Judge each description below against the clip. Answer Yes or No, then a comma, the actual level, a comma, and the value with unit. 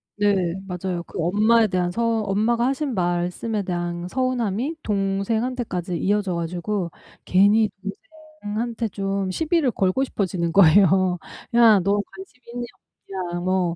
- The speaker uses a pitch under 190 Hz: No, high, 200 Hz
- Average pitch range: Yes, average, 4.3 semitones